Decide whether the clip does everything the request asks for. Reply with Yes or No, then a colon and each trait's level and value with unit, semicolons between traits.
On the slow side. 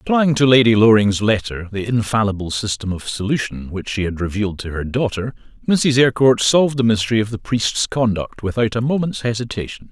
No: average, 180 wpm